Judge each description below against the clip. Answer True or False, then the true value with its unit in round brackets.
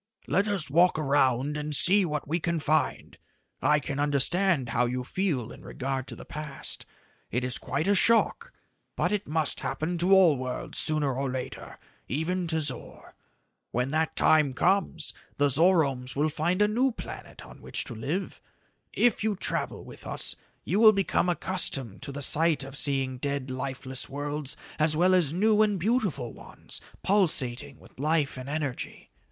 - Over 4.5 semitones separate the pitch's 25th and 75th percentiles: True (5.0 semitones)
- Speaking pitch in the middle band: True (150 Hz)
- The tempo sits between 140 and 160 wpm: False (170 wpm)